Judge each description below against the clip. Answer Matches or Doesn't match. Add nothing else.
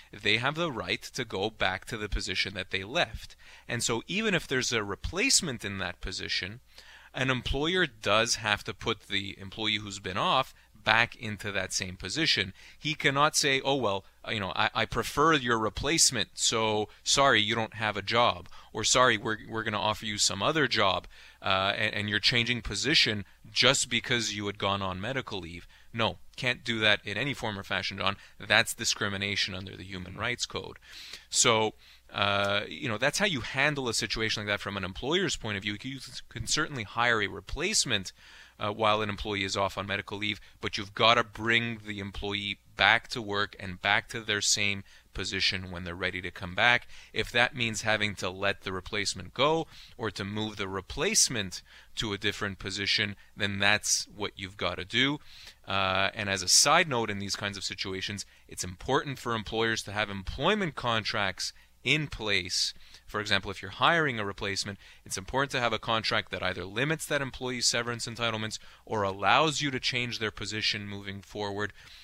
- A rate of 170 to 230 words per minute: Matches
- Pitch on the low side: Matches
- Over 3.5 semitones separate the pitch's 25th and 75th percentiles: Doesn't match